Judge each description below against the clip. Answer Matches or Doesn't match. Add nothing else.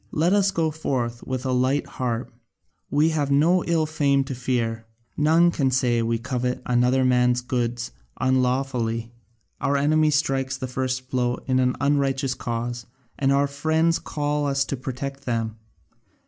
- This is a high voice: Doesn't match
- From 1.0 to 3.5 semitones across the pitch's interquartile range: Matches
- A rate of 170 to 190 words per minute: Doesn't match